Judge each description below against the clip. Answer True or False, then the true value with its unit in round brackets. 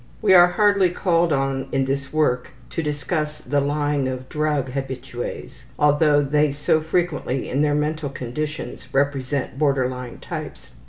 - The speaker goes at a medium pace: True (150 wpm)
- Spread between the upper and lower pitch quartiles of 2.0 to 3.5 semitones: True (2.4 semitones)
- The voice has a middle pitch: True (145 Hz)